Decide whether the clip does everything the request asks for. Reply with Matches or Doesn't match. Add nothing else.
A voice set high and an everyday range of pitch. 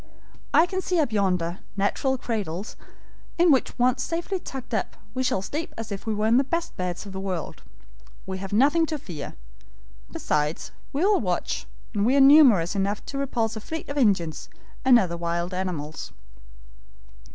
Doesn't match